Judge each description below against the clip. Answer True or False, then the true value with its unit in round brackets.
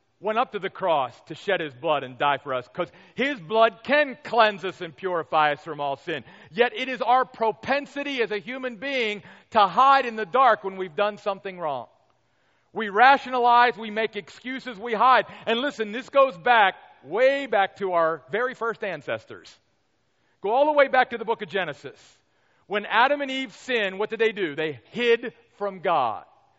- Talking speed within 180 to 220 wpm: True (195 wpm)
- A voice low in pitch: False (220 Hz)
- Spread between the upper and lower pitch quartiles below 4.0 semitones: False (5.4 semitones)